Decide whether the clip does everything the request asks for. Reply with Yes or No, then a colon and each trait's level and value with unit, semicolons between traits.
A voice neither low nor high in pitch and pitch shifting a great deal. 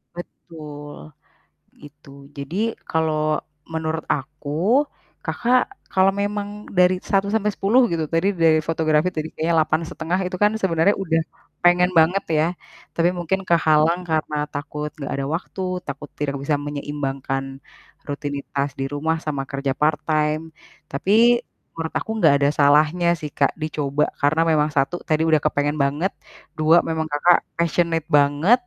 No: medium, 155 Hz; average, 2.7 semitones